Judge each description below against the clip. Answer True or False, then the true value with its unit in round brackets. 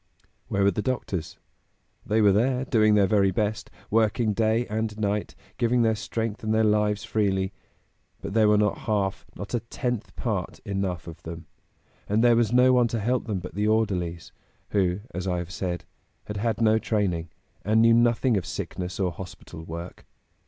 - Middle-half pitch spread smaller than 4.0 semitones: True (2.9 semitones)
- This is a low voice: True (105 Hz)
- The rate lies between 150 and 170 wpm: False (185 wpm)